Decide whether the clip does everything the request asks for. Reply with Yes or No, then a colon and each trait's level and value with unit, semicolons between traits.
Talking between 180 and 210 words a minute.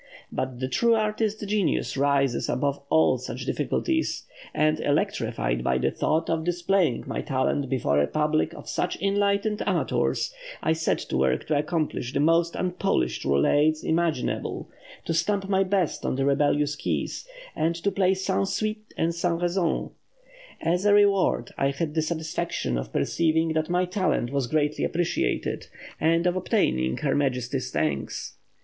No: average, 155 wpm